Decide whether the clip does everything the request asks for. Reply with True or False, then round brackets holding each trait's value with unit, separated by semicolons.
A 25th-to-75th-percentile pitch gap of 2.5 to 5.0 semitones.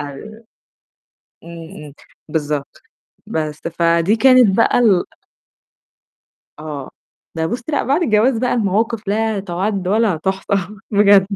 False (5.4 semitones)